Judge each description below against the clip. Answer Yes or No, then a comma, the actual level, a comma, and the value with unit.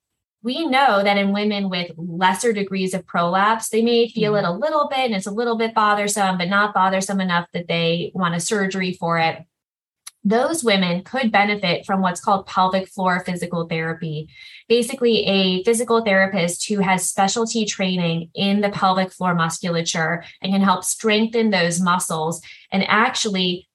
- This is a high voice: Yes, high, 195 Hz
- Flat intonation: No, average, 3.4 semitones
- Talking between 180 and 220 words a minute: No, average, 165 wpm